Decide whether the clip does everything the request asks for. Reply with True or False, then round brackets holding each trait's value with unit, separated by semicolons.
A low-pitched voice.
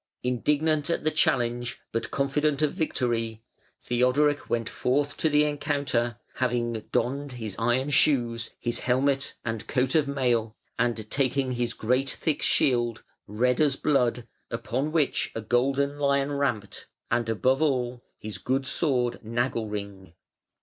True (125 Hz)